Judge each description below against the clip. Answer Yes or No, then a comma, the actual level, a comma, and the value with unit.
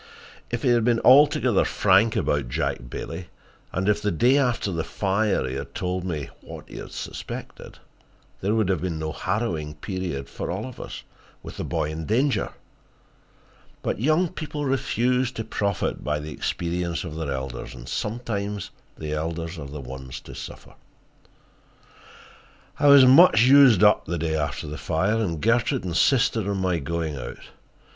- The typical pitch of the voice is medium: No, very low, 95 Hz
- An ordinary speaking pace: Yes, average, 165 wpm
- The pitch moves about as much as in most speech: No, wide, 6.9 semitones